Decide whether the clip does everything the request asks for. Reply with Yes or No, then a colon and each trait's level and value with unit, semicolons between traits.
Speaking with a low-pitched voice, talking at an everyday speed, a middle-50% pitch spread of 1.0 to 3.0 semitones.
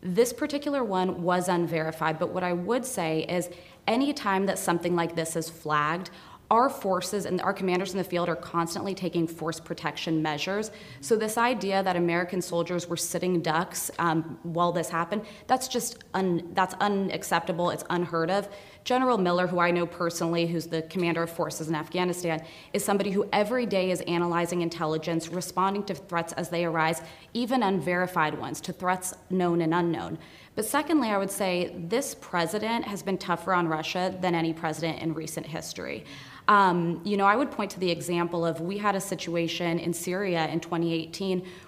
No: medium, 175 Hz; average, 180 wpm; narrow, 2.5 semitones